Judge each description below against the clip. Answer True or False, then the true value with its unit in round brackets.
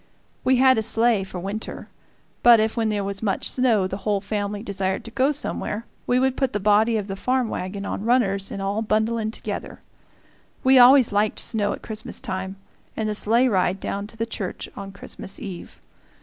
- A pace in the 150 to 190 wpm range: False (200 wpm)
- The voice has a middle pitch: False (215 Hz)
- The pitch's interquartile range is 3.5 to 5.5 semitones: False (2.9 semitones)